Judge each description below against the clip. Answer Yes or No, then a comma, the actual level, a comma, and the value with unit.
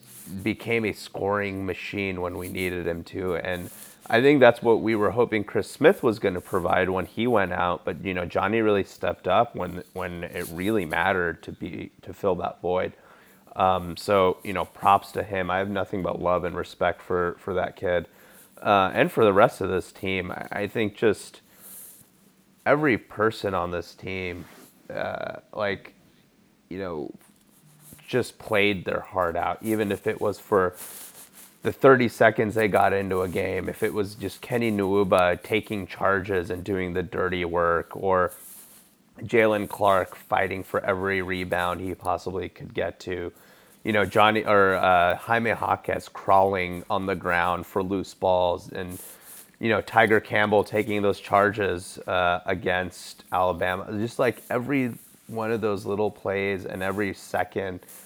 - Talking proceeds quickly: No, average, 170 wpm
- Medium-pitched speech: No, very low, 95 Hz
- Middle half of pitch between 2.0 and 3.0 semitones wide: Yes, narrow, 2.6 semitones